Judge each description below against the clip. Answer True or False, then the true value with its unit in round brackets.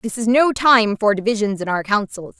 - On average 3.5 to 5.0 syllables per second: False (5.2 syllables/s)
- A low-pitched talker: False (215 Hz)